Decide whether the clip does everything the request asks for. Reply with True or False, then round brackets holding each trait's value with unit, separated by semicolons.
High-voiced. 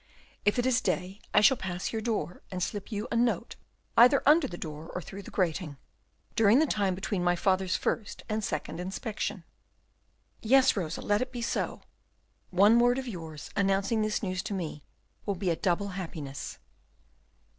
True (200 Hz)